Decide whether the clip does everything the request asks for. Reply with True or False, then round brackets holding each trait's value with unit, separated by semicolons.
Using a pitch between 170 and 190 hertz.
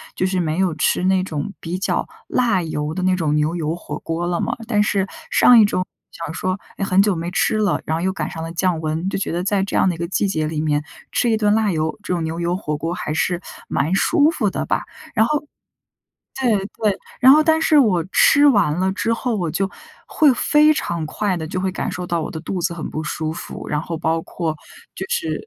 True (185 Hz)